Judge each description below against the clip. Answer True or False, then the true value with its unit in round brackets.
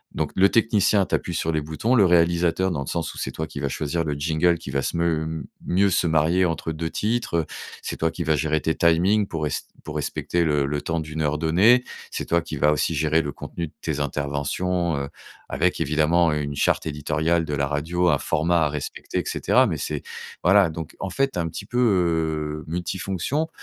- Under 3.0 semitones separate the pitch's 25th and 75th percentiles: True (2.6 semitones)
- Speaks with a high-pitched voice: False (80 Hz)